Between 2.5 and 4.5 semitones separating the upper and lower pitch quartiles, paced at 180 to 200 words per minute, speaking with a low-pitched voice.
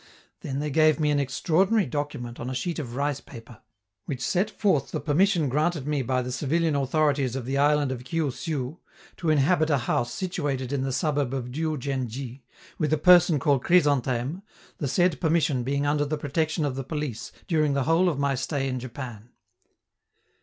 No: average, 3.2 semitones; average, 190 wpm; medium, 145 Hz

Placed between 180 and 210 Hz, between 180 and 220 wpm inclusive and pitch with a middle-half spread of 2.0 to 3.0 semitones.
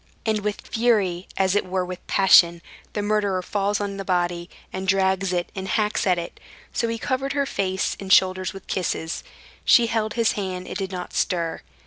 Yes: high, 190 Hz; average, 190 wpm; narrow, 2.4 semitones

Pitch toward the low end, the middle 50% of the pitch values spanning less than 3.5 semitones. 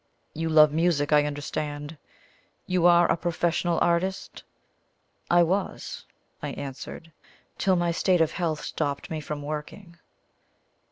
No: medium, 165 Hz; narrow, 2.6 semitones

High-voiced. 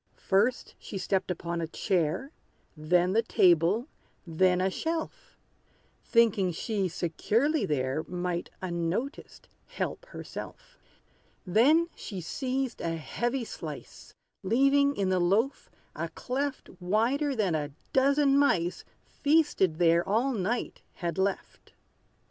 Yes: high, 200 Hz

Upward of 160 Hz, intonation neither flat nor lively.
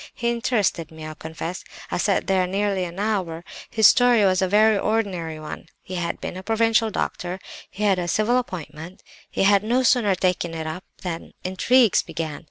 Yes: high, 190 Hz; average, 4.1 semitones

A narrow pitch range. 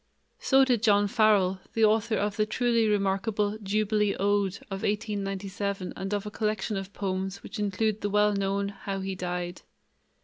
Yes: narrow, 1.7 semitones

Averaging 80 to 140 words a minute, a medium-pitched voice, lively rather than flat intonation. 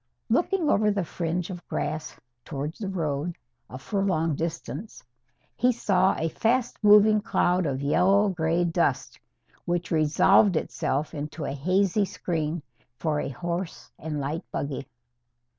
No: slow, 135 wpm; medium, 170 Hz; average, 4.2 semitones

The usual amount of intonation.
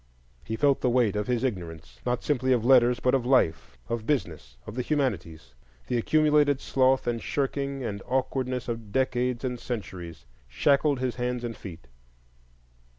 Yes: average, 4.0 semitones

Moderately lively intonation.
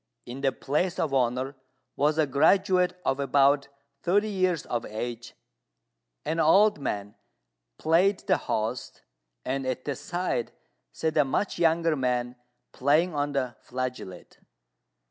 Yes: average, 4.8 semitones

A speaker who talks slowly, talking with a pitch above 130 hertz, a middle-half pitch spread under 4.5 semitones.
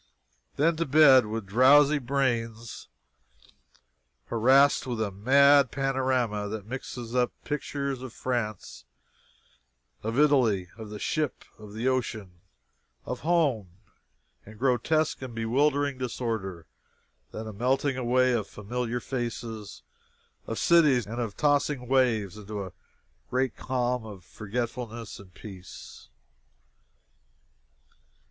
No: slow, 110 wpm; low, 120 Hz; average, 3.7 semitones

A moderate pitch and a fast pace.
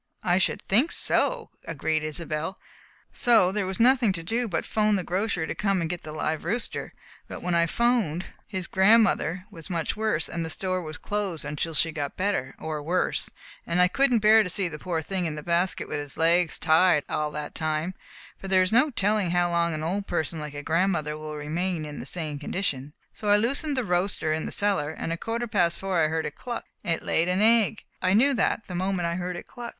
Yes: medium, 180 Hz; fast, 230 wpm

